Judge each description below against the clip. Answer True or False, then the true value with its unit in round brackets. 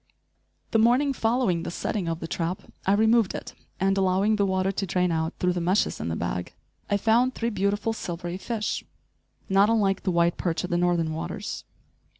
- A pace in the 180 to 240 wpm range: True (195 wpm)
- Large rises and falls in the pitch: False (3.9 semitones)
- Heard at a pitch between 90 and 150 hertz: False (190 Hz)